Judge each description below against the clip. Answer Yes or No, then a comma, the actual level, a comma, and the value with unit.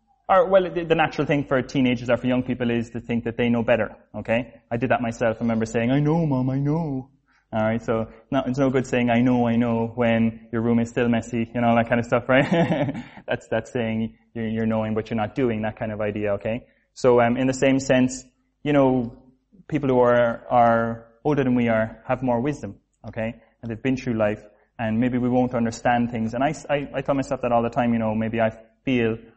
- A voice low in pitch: Yes, low, 120 Hz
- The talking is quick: Yes, fast, 235 wpm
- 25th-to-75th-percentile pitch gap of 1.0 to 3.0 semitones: Yes, narrow, 2.4 semitones